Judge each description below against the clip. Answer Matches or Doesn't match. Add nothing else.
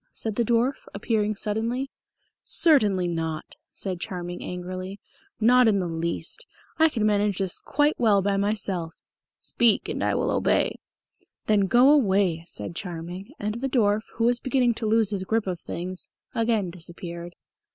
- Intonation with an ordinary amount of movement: Matches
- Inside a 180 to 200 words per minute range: Doesn't match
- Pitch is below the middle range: Doesn't match